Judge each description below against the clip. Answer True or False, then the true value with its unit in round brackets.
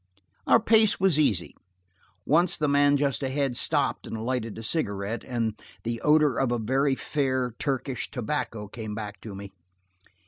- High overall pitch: False (130 Hz)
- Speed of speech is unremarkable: True (160 wpm)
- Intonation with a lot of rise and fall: False (4.4 semitones)